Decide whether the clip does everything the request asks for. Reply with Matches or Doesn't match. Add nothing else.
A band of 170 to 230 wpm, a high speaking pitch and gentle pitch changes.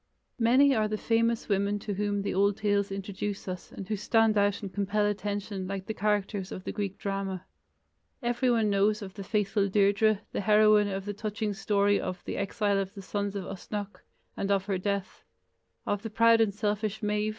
Matches